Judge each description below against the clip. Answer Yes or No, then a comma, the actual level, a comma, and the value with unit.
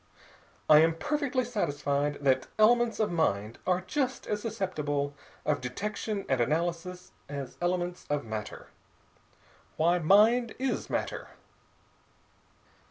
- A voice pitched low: No, medium, 175 Hz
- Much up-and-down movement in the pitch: Yes, wide, 6.9 semitones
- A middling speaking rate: No, slow, 110 wpm